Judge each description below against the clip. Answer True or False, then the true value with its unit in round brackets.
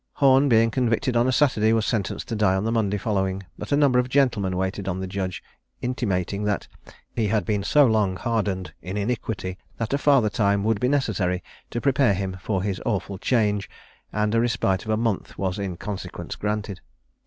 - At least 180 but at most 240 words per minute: True (200 wpm)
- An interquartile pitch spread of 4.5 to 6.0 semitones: False (3.5 semitones)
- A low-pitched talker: True (105 Hz)